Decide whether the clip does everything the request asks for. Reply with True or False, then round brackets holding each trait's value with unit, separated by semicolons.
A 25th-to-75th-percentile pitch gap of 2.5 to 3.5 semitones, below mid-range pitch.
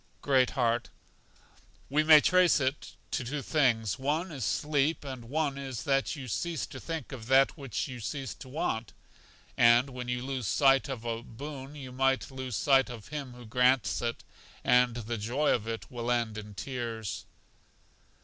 True (2.9 semitones; 130 Hz)